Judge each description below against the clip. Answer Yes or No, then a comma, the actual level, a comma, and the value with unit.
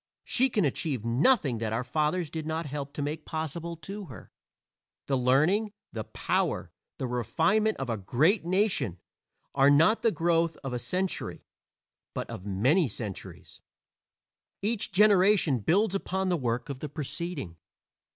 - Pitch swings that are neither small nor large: No, wide, 6.5 semitones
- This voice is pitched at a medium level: Yes, medium, 155 Hz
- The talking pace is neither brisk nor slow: Yes, average, 150 wpm